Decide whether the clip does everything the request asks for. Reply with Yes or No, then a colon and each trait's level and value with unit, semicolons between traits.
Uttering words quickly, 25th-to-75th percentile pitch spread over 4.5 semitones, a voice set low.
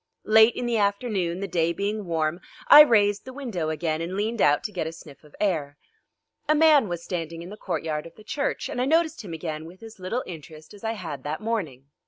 No: fast, 230 wpm; wide, 5.6 semitones; medium, 185 Hz